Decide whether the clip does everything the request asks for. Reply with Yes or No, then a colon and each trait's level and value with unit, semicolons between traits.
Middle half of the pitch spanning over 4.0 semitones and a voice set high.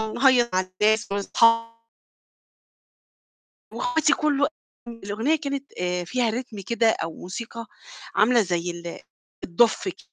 Yes: average, 4.6 semitones; high, 230 Hz